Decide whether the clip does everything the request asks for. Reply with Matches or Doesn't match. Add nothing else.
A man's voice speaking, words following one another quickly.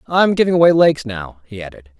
Matches